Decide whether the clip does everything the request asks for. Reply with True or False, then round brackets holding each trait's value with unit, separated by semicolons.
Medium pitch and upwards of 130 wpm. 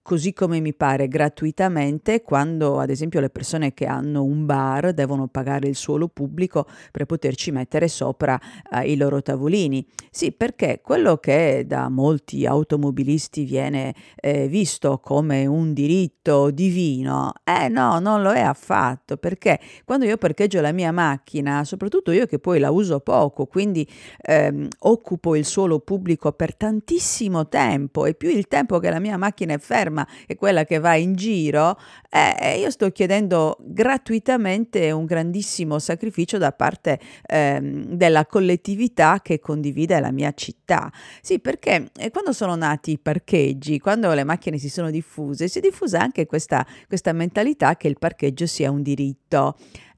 True (155 Hz; 155 wpm)